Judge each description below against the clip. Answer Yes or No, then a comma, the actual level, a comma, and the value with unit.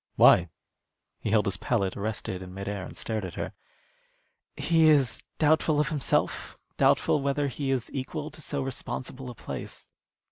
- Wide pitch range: Yes, wide, 5.9 semitones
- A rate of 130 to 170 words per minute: Yes, average, 165 wpm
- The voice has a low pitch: Yes, low, 130 Hz